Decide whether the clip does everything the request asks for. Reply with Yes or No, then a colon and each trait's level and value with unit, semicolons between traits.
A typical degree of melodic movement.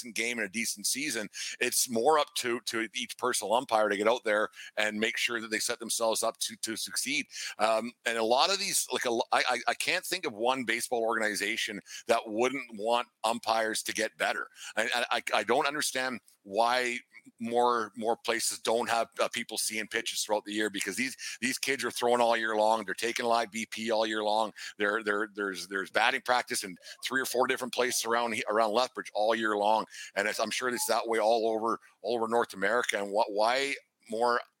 No: narrow, 1.8 semitones